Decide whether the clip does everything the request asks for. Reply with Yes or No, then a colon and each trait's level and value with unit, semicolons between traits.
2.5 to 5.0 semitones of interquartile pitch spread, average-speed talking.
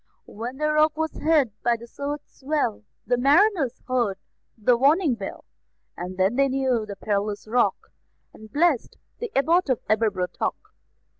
No: wide, 5.6 semitones; average, 150 wpm